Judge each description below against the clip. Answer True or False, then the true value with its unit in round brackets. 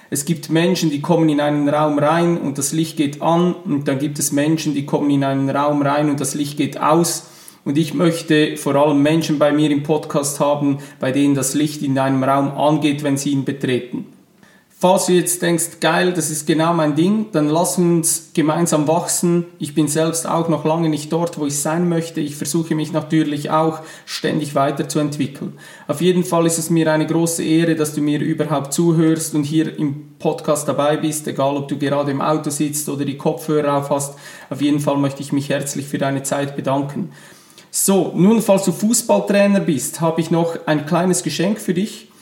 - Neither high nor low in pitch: True (155 Hz)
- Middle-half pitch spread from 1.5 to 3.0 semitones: True (2.5 semitones)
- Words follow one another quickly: True (205 wpm)